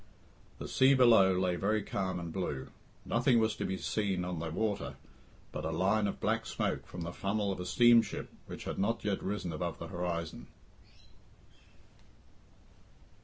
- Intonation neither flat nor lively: Yes, average, 3.7 semitones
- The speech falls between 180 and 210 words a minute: No, average, 165 wpm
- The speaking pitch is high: No, very low, 95 Hz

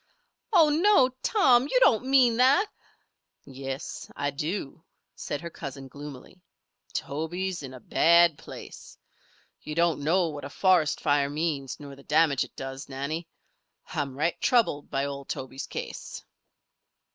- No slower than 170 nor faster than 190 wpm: No, average, 140 wpm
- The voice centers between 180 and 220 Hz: No, medium, 150 Hz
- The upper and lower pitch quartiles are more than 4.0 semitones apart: Yes, average, 5.2 semitones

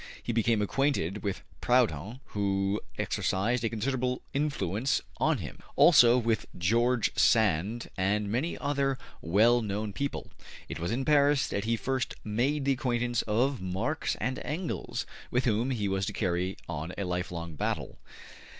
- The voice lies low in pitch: Yes, low, 115 Hz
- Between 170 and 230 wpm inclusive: No, average, 150 wpm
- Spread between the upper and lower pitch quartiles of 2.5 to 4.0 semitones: No, average, 4.6 semitones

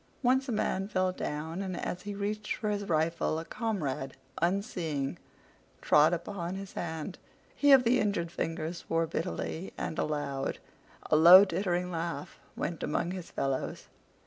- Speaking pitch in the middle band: Yes, medium, 175 Hz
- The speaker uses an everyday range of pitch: Yes, average, 3.8 semitones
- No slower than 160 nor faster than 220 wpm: No, average, 150 wpm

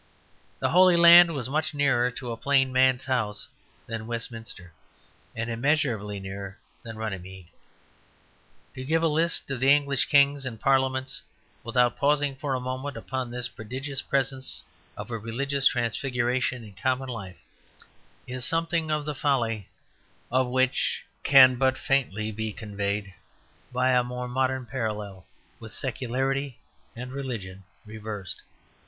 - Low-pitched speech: Yes, low, 130 Hz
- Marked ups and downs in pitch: No, average, 3.4 semitones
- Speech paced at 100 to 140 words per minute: Yes, slow, 135 wpm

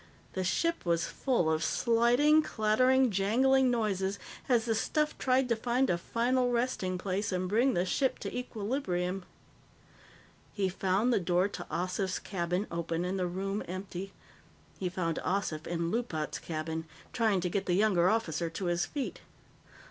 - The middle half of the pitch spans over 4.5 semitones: Yes, average, 5.1 semitones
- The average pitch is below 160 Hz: No, high, 195 Hz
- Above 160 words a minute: No, average, 155 wpm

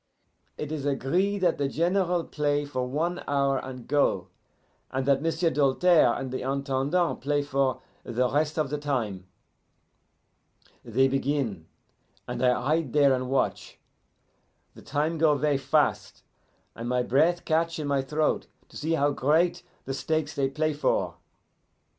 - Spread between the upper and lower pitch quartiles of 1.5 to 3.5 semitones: Yes, average, 2.9 semitones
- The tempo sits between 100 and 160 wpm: Yes, average, 150 wpm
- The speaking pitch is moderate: Yes, medium, 145 Hz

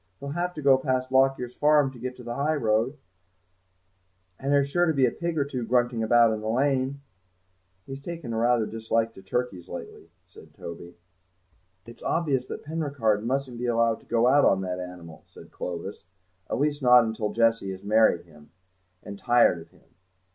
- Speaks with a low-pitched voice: Yes, low, 120 Hz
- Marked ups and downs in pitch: No, average, 4.0 semitones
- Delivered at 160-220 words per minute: Yes, average, 190 wpm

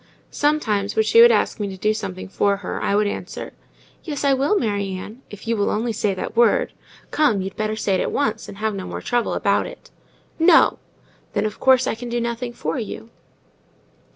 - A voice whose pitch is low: No, high, 220 Hz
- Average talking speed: No, fast, 210 wpm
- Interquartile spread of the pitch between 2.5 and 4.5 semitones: Yes, average, 3.2 semitones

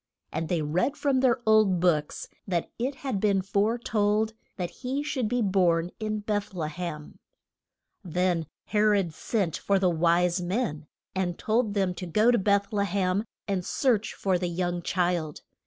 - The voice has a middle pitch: No, high, 195 Hz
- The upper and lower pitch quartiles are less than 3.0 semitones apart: No, average, 3.6 semitones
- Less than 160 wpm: No, average, 170 wpm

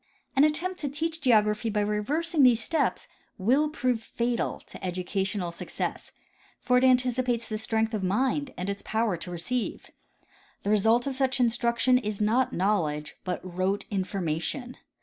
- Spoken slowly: No, average, 155 wpm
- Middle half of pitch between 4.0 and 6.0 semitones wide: Yes, average, 4.5 semitones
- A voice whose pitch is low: No, high, 230 Hz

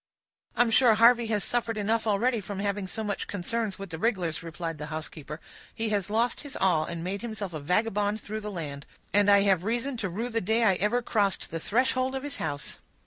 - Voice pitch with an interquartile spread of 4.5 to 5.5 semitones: No, average, 4.1 semitones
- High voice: Yes, high, 205 Hz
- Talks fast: Yes, fast, 215 wpm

